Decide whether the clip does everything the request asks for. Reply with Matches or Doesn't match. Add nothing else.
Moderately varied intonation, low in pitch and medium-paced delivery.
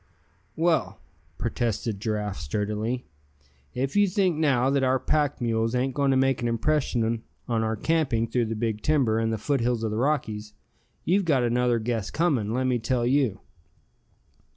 Matches